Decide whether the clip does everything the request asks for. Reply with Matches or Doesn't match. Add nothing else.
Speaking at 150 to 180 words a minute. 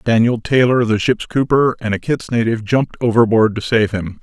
Doesn't match